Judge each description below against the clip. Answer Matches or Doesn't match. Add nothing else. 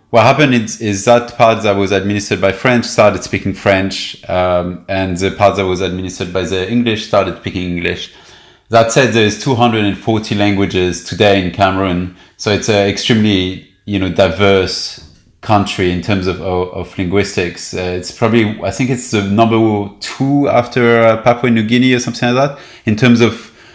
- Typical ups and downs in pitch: Matches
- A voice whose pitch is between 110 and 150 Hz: Doesn't match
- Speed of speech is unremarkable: Matches